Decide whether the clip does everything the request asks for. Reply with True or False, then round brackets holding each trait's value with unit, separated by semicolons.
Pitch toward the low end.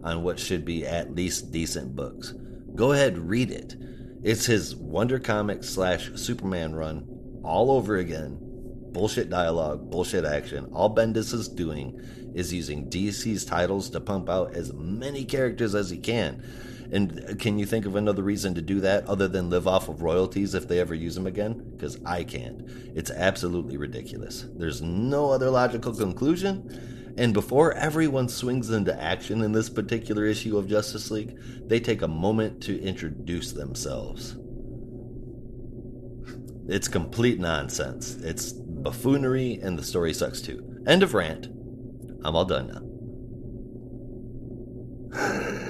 True (115 Hz)